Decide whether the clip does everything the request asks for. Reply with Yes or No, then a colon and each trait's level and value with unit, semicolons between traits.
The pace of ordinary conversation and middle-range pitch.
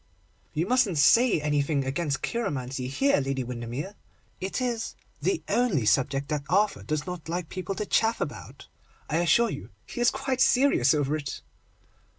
Yes: average, 160 wpm; medium, 160 Hz